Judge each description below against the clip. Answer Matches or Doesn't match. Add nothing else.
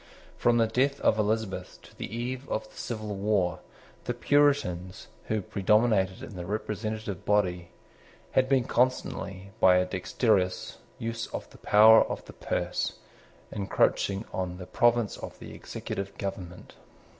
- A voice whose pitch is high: Doesn't match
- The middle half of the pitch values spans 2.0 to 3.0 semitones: Doesn't match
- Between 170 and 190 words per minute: Doesn't match